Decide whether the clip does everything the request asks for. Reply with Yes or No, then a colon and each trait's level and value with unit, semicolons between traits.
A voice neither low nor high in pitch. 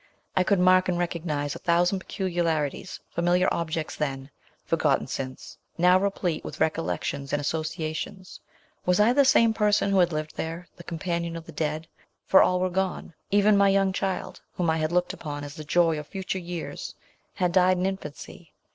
Yes: medium, 175 Hz